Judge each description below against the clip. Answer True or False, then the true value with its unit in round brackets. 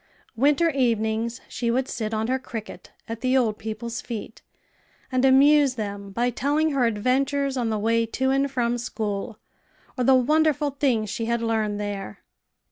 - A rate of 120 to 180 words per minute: True (165 wpm)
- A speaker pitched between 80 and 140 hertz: False (235 Hz)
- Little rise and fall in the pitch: False (3.4 semitones)